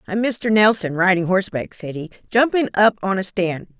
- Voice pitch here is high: Yes, high, 195 Hz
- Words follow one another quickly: No, average, 190 wpm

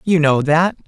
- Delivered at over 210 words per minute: No, fast, 205 wpm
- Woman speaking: No, male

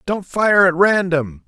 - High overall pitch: No, medium, 180 Hz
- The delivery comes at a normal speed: Yes, average, 165 wpm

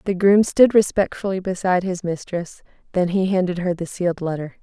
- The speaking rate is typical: Yes, average, 180 wpm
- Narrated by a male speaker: No, female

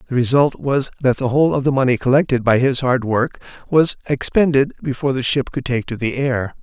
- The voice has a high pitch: No, low, 130 Hz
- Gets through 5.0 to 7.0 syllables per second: Yes, 5.7 syllables/s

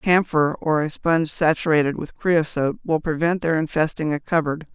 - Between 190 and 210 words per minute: No, average, 165 wpm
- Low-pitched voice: No, medium, 160 Hz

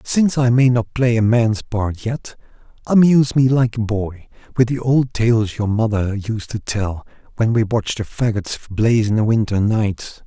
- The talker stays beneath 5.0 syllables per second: Yes, 4.6 syllables/s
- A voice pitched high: No, low, 115 Hz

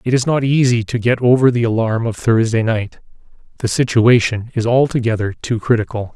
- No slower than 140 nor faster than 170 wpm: Yes, average, 165 wpm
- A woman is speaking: No, male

